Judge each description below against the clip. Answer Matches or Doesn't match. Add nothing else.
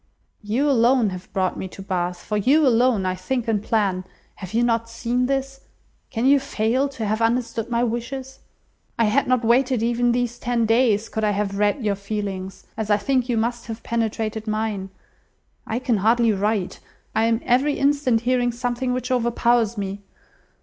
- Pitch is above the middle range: Matches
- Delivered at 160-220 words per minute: Matches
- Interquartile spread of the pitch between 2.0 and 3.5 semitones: Matches